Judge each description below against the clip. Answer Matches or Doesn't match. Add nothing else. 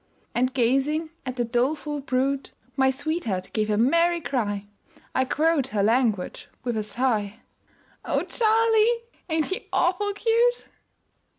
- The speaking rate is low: Matches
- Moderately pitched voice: Doesn't match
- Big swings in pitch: Matches